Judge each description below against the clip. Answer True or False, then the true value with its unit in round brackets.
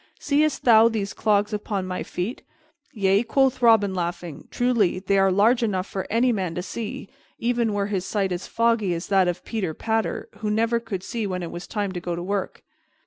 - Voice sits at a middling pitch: False (205 Hz)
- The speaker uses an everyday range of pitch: True (3.6 semitones)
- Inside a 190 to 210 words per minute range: True (200 wpm)